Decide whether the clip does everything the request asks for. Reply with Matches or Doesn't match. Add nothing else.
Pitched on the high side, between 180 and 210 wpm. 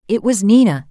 Matches